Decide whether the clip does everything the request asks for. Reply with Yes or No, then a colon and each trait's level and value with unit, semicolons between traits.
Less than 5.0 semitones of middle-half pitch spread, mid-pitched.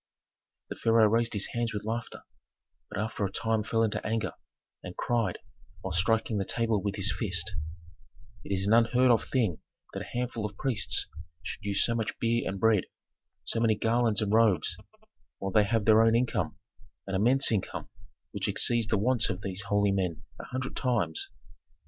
No: narrow, 2.6 semitones; low, 110 Hz